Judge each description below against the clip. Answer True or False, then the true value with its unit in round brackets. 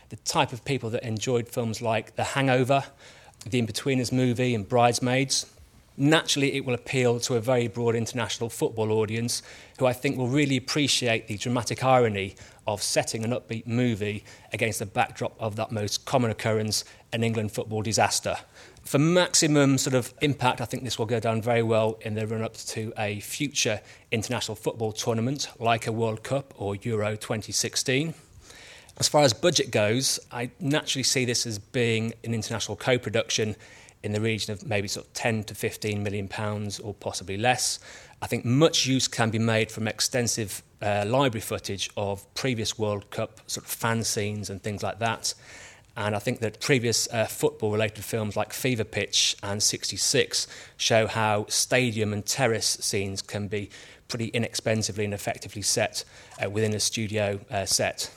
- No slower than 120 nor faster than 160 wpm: False (175 wpm)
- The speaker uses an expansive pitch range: False (2.9 semitones)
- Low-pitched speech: True (115 Hz)